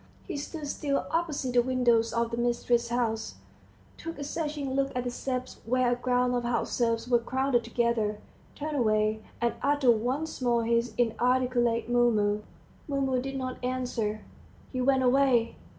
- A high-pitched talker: Yes, high, 245 Hz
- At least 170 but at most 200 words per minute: No, average, 160 wpm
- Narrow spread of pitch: Yes, narrow, 2.1 semitones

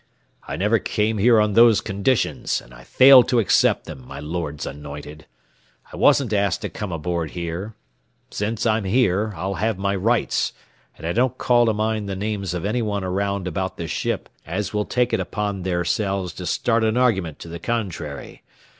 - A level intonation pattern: No, average, 4.1 semitones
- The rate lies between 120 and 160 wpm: No, average, 185 wpm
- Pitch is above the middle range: No, low, 100 Hz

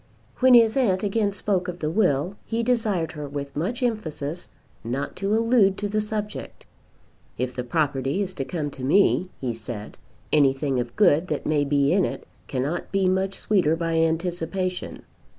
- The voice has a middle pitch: Yes, medium, 175 Hz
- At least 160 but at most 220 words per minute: Yes, average, 170 wpm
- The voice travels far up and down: Yes, wide, 6.0 semitones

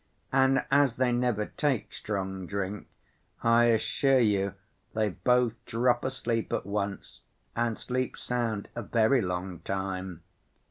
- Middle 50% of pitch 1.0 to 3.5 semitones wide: No, average, 4.0 semitones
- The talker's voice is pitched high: No, low, 115 Hz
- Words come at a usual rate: No, slow, 130 wpm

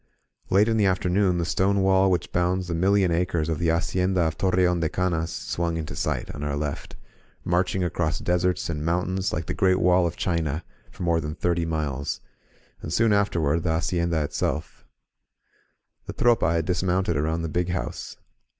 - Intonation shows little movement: Yes, narrow, 2.2 semitones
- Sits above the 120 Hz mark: No, very low, 85 Hz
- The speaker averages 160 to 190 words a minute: Yes, average, 175 wpm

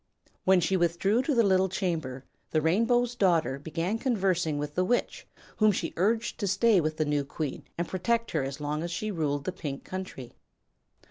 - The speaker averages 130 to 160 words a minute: No, average, 190 wpm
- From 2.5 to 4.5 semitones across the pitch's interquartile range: No, average, 5.0 semitones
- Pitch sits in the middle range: Yes, medium, 180 Hz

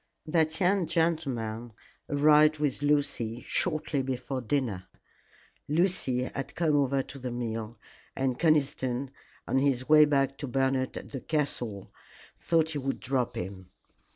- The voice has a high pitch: No, low, 135 Hz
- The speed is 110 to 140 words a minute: Yes, slow, 135 wpm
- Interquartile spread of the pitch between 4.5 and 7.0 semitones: No, average, 3.5 semitones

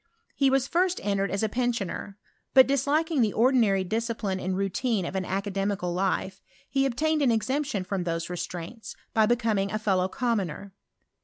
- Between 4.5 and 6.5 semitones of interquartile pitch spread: Yes, average, 4.8 semitones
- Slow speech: No, average, 160 wpm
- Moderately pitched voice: No, high, 210 Hz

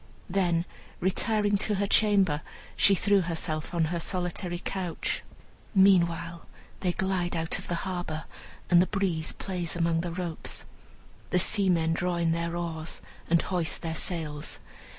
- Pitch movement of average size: No, narrow, 2.3 semitones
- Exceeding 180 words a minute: No, average, 145 wpm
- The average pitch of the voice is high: No, medium, 175 Hz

